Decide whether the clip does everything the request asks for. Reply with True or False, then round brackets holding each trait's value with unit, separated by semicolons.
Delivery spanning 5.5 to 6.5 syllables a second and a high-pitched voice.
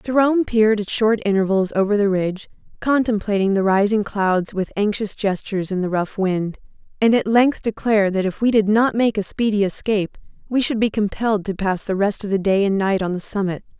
True (5.6 syllables/s; 205 Hz)